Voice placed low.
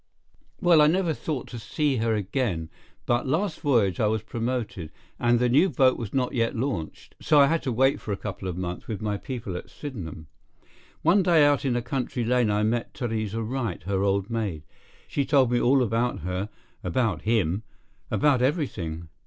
Yes: low, 120 Hz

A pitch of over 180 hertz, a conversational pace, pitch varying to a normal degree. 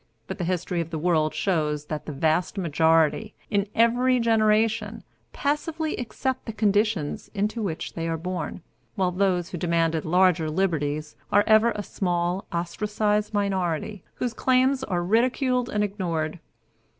Yes: high, 190 Hz; average, 145 wpm; average, 4.7 semitones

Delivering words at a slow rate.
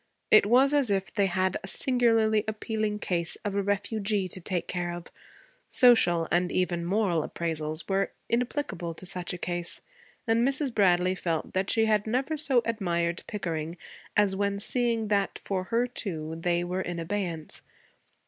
No: average, 165 wpm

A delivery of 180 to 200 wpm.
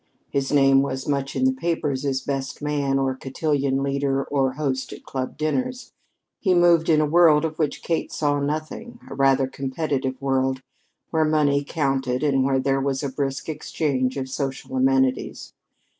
No: average, 170 wpm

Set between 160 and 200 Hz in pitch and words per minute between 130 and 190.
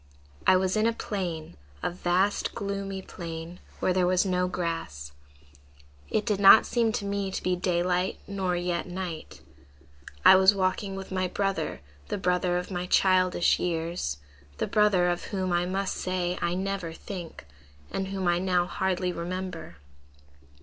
Yes: medium, 185 Hz; average, 155 wpm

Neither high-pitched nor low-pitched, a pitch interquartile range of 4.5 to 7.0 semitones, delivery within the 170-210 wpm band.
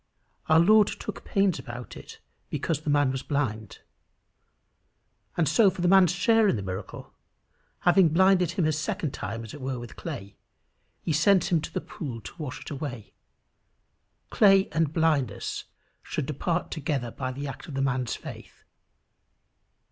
No: medium, 150 Hz; average, 5.3 semitones; average, 160 wpm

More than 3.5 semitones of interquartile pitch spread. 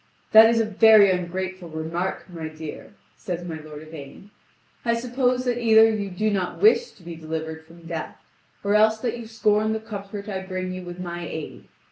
Yes: average, 4.6 semitones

